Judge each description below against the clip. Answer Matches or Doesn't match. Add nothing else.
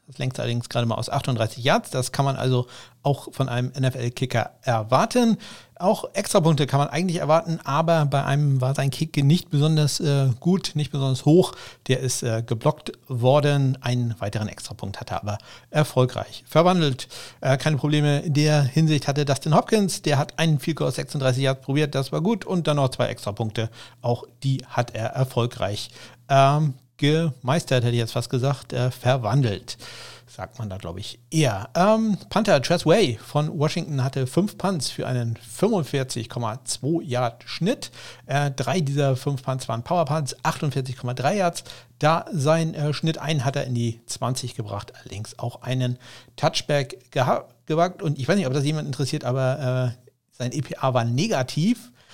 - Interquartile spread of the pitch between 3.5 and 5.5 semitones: Matches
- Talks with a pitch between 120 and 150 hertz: Matches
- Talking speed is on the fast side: Doesn't match